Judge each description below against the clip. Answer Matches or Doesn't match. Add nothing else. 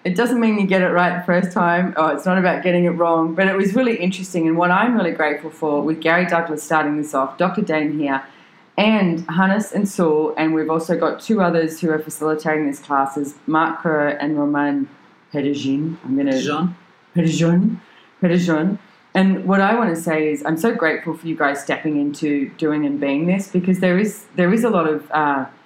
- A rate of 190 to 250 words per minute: Matches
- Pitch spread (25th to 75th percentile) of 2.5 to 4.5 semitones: Matches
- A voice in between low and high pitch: Matches